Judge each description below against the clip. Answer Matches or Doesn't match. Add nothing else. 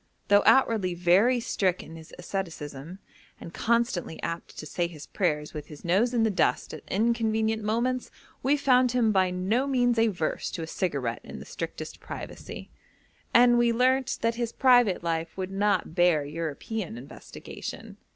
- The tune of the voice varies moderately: Doesn't match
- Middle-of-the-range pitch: Doesn't match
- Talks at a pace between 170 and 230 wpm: Doesn't match